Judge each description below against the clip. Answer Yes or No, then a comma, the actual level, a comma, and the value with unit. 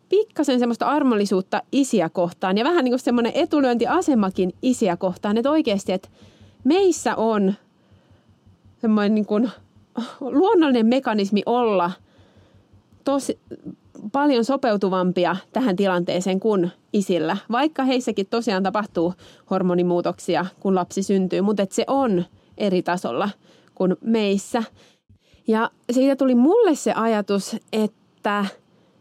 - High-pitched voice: Yes, high, 210 Hz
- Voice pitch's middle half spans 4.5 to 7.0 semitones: Yes, average, 5.2 semitones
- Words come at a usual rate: Yes, average, 110 wpm